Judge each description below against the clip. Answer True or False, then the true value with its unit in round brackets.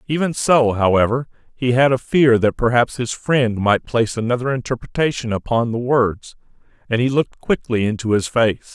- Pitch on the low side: True (120 Hz)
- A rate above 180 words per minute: False (170 wpm)